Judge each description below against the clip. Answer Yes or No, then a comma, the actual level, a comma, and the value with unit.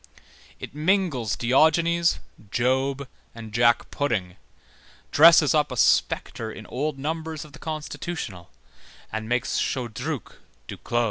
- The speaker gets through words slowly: Yes, slow, 115 wpm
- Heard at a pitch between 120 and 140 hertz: Yes, low, 135 Hz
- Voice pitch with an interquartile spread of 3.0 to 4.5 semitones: No, average, 5.0 semitones